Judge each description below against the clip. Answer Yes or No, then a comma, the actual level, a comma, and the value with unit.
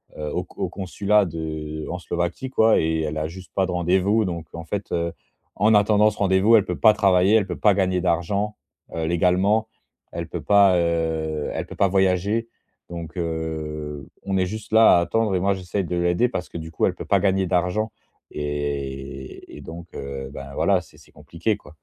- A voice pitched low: Yes, very low, 90 Hz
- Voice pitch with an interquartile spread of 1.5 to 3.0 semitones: No, average, 3.7 semitones